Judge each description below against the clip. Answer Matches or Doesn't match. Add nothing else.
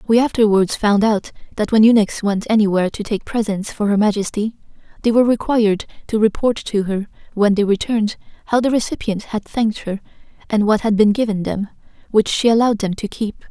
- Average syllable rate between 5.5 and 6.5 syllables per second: Matches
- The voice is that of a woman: Matches